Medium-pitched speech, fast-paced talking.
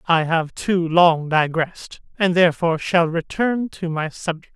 No: medium, 170 Hz; average, 160 wpm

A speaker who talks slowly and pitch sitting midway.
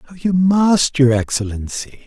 Yes: slow, 115 wpm; medium, 145 Hz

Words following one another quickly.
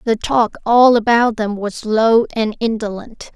No: average, 160 wpm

